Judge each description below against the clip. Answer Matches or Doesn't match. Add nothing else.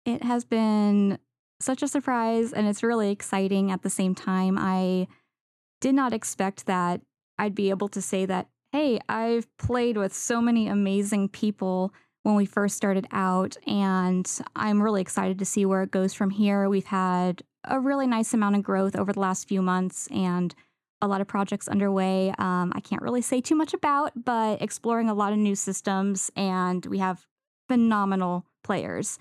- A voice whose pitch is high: Matches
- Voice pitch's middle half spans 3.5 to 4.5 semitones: Doesn't match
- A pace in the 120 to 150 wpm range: Doesn't match